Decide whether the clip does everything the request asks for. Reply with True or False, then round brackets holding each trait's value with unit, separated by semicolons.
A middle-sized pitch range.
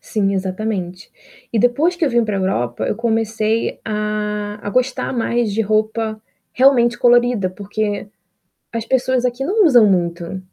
True (3.0 semitones)